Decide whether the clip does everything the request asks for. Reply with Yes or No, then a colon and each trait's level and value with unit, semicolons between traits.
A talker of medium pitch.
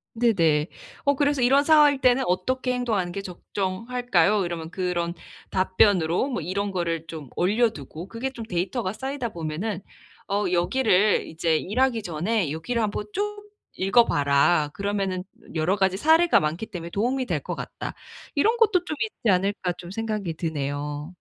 No: high, 195 Hz